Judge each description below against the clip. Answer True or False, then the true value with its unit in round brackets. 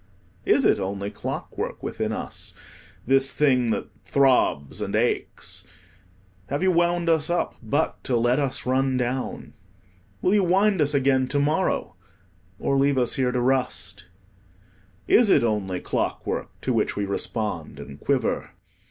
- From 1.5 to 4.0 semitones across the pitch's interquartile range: False (4.6 semitones)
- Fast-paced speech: False (145 wpm)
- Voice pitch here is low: True (130 Hz)